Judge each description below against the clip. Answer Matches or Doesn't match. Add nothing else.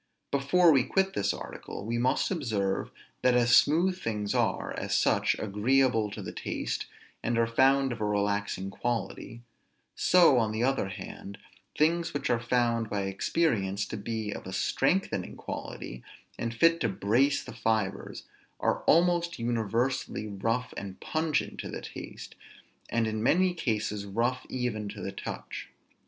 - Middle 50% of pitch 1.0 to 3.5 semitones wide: Doesn't match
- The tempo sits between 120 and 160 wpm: Matches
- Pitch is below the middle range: Matches